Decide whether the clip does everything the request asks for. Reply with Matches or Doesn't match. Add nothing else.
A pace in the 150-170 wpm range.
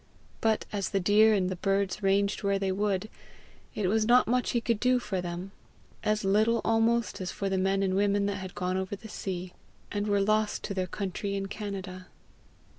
Doesn't match